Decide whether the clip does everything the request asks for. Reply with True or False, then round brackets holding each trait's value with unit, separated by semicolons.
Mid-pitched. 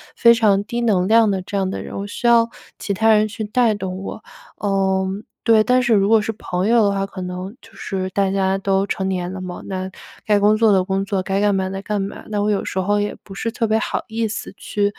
False (200 Hz)